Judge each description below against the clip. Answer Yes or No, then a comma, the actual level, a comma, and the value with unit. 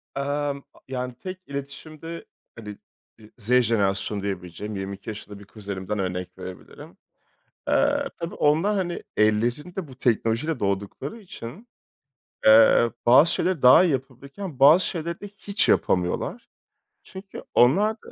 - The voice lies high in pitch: No, low, 130 Hz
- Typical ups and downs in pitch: No, wide, 7.8 semitones